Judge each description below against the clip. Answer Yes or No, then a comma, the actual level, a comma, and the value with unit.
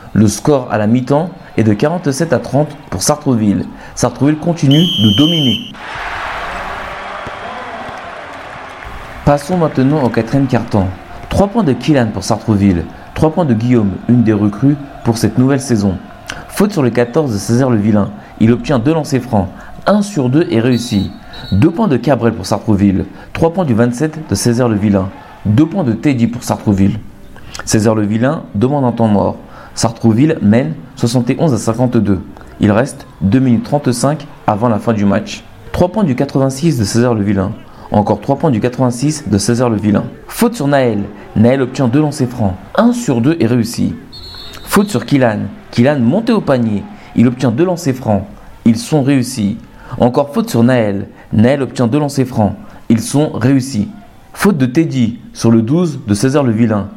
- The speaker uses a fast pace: No, average, 170 wpm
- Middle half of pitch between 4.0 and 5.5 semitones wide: Yes, average, 4.9 semitones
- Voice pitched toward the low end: Yes, low, 120 Hz